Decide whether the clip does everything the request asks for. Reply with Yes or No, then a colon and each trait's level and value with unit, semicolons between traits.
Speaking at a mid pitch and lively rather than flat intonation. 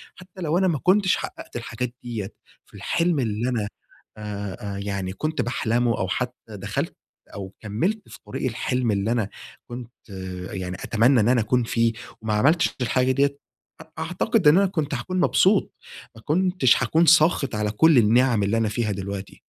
No: low, 120 Hz; wide, 6.7 semitones